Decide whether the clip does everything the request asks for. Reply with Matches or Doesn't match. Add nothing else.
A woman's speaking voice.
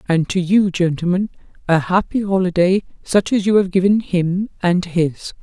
Matches